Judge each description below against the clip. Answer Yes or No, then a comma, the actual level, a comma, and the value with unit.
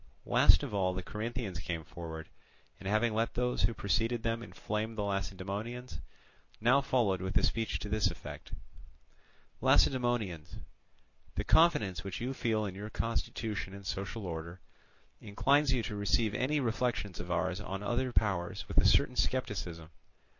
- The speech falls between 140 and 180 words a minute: Yes, average, 155 wpm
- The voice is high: No, low, 105 Hz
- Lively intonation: No, average, 4.1 semitones